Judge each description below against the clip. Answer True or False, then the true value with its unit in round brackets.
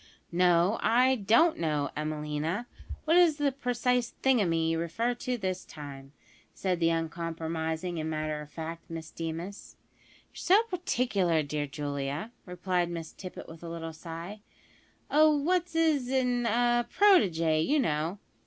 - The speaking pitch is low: False (175 Hz)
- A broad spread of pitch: True (7.4 semitones)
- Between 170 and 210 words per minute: False (145 wpm)